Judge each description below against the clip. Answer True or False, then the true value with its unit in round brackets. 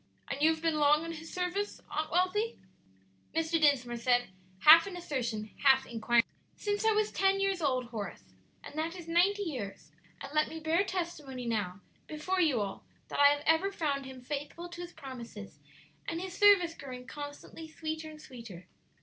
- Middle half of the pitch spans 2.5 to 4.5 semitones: False (5.4 semitones)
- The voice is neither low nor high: False (310 Hz)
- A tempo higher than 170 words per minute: True (180 wpm)